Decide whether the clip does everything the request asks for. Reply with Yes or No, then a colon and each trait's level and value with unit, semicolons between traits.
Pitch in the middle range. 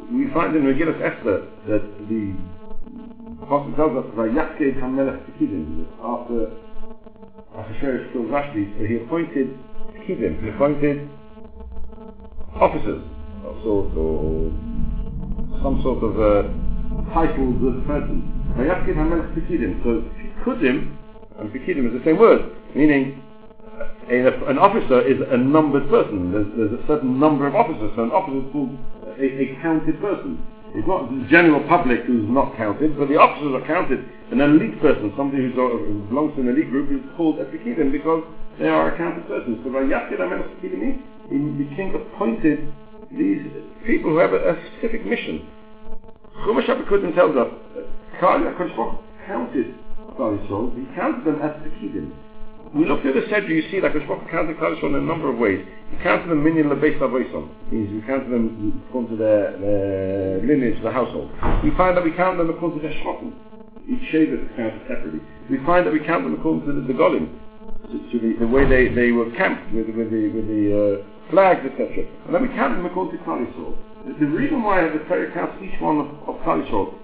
Yes: medium, 145 Hz